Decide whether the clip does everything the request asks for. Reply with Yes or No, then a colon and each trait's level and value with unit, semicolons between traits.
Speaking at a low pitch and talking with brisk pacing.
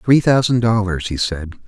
No: low, 105 Hz; average, 180 wpm